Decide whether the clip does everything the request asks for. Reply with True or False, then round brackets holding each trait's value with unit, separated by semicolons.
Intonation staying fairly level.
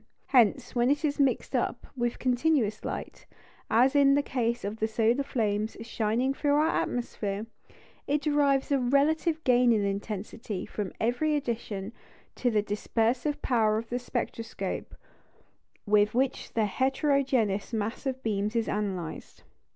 False (4.2 semitones)